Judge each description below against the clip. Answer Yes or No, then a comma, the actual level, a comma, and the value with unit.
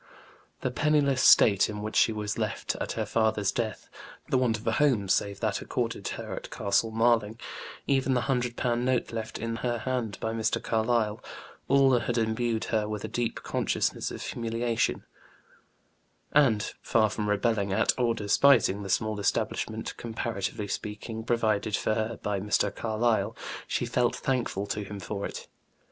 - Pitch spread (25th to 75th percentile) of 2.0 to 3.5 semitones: Yes, narrow, 2.4 semitones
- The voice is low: Yes, low, 110 Hz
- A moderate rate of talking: Yes, average, 165 wpm